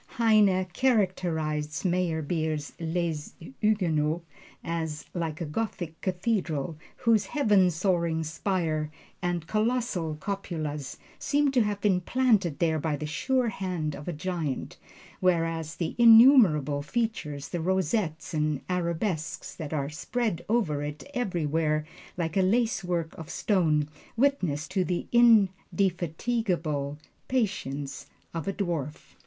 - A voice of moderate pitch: Yes, medium, 175 Hz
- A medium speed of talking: No, slow, 115 wpm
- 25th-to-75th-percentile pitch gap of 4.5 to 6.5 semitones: Yes, average, 4.8 semitones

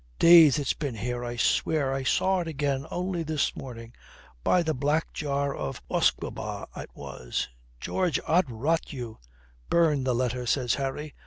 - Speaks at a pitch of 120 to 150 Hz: Yes, medium, 140 Hz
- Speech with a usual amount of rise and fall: Yes, average, 4.3 semitones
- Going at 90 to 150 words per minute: No, average, 165 wpm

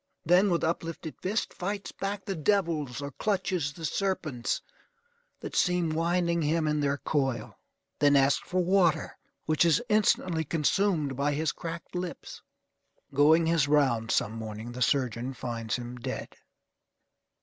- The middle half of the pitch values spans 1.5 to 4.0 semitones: No, average, 4.5 semitones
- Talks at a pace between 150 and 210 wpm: No, average, 140 wpm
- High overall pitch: No, medium, 155 Hz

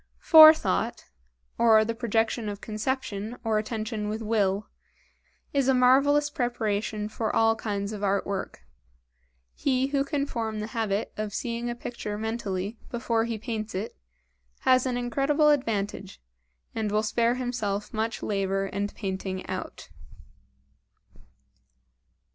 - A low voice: No, high, 225 Hz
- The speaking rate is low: Yes, slow, 130 wpm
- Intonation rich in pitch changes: No, average, 2.9 semitones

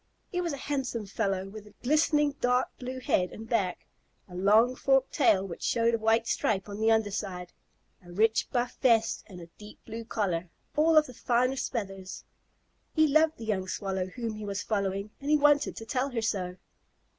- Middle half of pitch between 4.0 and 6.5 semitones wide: Yes, average, 4.6 semitones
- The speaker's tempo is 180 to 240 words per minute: Yes, average, 195 wpm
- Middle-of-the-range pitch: No, high, 225 Hz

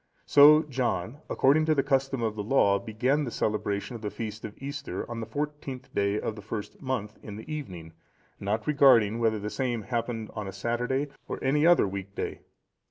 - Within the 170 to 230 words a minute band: Yes, average, 195 wpm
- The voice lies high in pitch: No, low, 115 Hz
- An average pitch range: Yes, average, 4.6 semitones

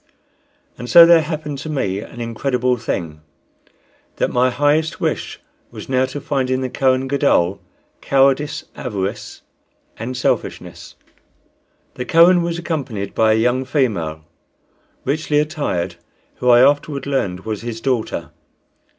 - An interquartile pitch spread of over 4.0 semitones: Yes, average, 4.6 semitones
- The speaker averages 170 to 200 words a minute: No, slow, 135 wpm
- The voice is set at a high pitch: No, low, 130 Hz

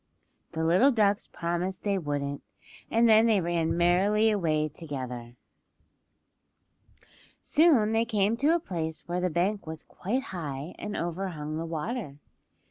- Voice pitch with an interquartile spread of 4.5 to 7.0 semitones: Yes, average, 5.0 semitones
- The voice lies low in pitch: No, medium, 180 Hz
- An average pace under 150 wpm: Yes, slow, 135 wpm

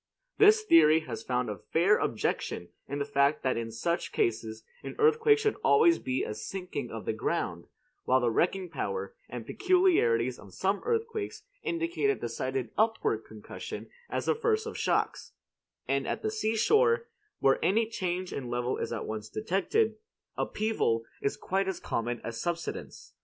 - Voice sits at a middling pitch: Yes, medium, 170 Hz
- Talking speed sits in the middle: Yes, average, 165 wpm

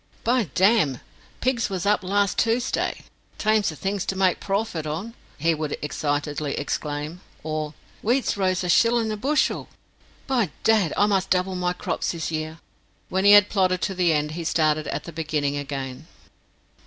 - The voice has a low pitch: No, medium, 180 Hz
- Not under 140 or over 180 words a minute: Yes, average, 165 wpm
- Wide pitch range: No, average, 4.9 semitones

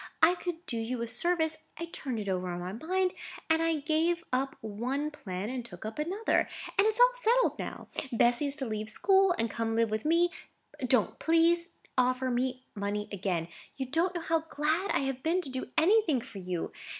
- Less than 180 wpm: No, fast, 205 wpm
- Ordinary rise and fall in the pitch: No, wide, 7.1 semitones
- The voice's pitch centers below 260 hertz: No, very high, 275 Hz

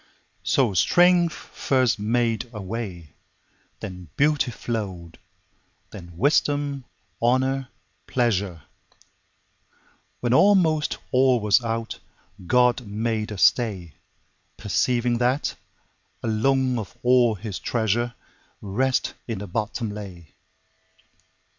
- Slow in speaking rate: Yes, slow, 85 wpm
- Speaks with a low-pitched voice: Yes, low, 115 Hz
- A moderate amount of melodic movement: Yes, average, 3.9 semitones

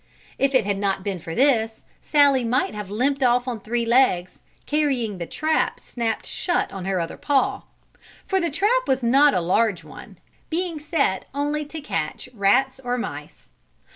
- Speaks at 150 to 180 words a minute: Yes, average, 170 wpm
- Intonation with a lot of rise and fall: Yes, wide, 5.9 semitones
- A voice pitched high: Yes, very high, 250 Hz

